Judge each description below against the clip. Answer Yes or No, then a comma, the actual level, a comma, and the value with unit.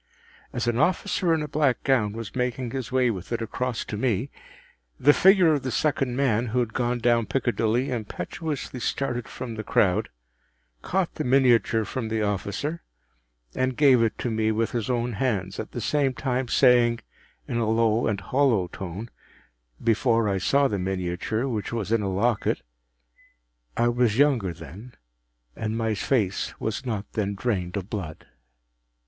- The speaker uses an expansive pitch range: No, average, 3.8 semitones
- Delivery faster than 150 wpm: Yes, average, 165 wpm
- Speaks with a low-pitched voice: Yes, low, 115 Hz